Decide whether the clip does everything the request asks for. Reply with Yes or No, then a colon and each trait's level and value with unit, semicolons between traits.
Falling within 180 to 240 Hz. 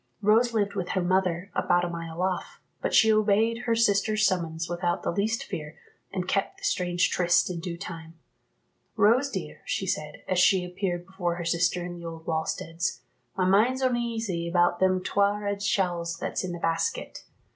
Yes: medium, 185 Hz